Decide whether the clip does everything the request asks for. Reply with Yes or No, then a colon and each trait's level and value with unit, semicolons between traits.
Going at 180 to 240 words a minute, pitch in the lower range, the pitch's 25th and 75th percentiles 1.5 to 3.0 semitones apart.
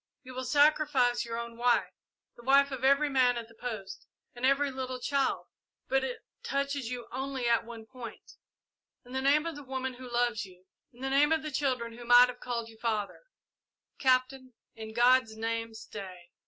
No: average, 190 wpm; very high, 250 Hz; narrow, 2.4 semitones